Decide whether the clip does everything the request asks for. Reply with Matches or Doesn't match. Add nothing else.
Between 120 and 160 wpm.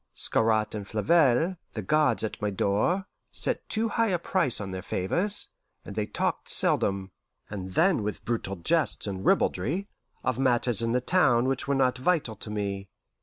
Doesn't match